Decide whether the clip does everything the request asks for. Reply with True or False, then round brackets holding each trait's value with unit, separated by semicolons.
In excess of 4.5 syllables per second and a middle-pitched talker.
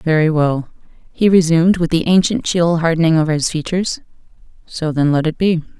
True (5.7 syllables/s; 165 Hz)